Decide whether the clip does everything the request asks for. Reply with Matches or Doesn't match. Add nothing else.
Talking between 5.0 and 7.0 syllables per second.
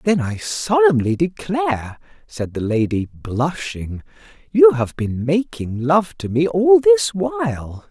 Doesn't match